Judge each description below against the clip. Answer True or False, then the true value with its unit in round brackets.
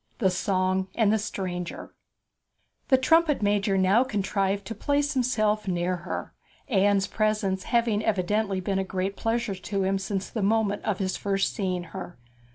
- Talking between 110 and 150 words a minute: False (160 wpm)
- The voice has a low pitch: False (200 Hz)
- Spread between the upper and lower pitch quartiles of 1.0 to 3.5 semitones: True (2.5 semitones)